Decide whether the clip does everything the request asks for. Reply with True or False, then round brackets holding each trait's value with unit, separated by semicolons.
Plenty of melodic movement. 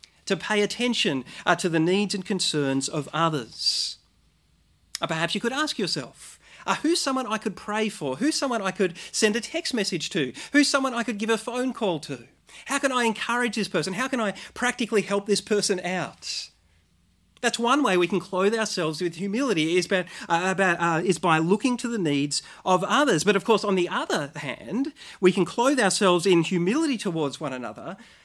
True (5.9 semitones)